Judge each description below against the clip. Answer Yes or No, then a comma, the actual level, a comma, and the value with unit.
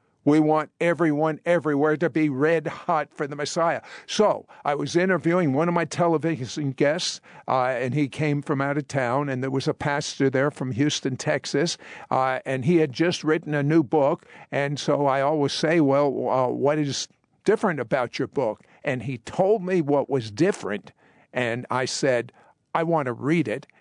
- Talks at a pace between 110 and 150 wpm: No, average, 185 wpm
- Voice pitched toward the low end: No, medium, 150 Hz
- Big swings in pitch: No, average, 3.0 semitones